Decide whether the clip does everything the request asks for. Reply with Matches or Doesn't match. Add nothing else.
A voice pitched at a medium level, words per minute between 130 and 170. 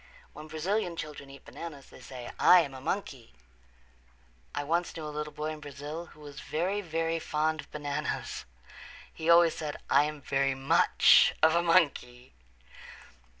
Matches